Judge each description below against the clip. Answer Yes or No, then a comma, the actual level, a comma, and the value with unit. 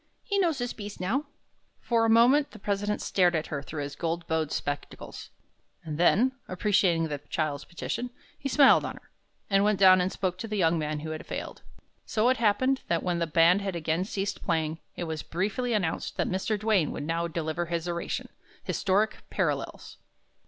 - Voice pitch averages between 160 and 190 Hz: Yes, medium, 185 Hz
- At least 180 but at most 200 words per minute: Yes, average, 190 wpm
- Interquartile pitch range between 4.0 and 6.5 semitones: Yes, average, 4.7 semitones